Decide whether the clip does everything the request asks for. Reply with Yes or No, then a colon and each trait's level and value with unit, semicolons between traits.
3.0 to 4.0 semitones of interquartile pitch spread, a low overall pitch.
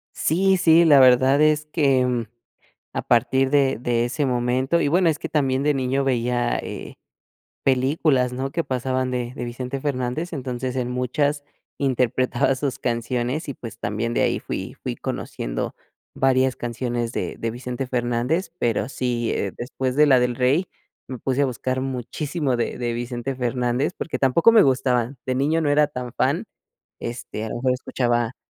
No: narrow, 2.4 semitones; low, 130 Hz